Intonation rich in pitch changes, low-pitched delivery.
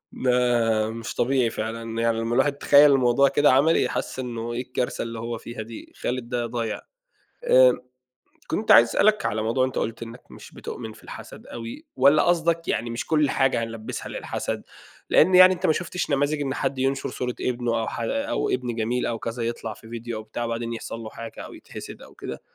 No: average, 3.2 semitones; low, 120 Hz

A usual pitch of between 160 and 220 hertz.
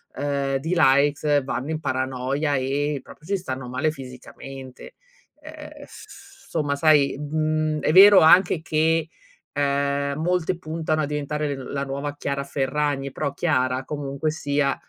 No: medium, 145 Hz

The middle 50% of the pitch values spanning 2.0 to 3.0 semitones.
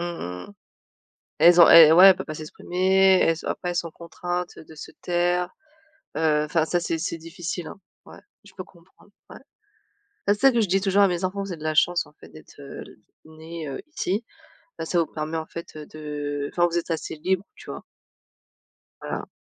Yes: average, 2.7 semitones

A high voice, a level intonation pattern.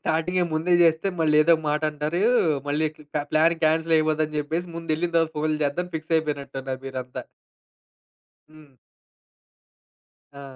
No: medium, 155 Hz; narrow, 1.5 semitones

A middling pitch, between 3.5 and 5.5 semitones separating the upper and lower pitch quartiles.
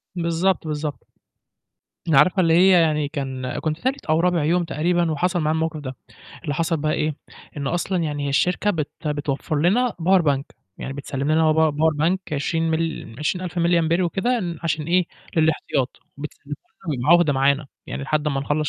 No: medium, 160 Hz; average, 2.8 semitones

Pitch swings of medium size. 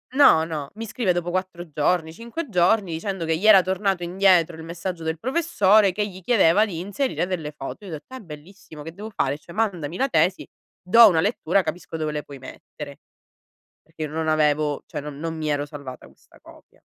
Yes: average, 4.1 semitones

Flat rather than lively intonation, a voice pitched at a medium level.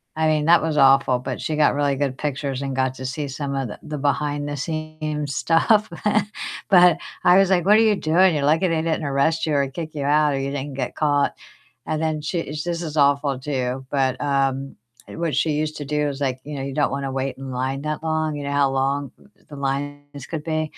Yes: narrow, 2.3 semitones; medium, 145 Hz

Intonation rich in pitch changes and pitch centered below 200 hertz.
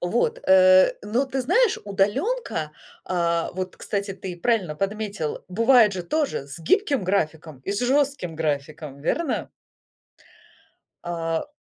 Yes: wide, 6.7 semitones; high, 190 Hz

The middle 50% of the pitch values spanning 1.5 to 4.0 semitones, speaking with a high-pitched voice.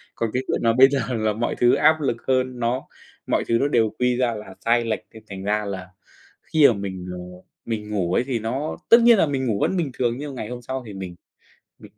No: average, 3.7 semitones; low, 120 Hz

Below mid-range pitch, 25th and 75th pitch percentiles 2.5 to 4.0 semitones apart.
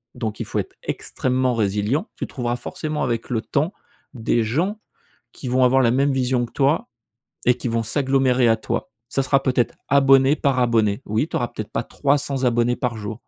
Yes: low, 125 Hz; average, 2.8 semitones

